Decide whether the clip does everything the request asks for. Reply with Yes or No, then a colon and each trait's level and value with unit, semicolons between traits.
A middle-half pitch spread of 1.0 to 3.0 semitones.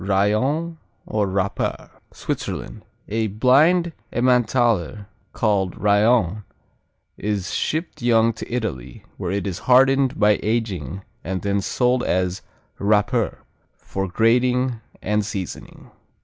No: average, 4.1 semitones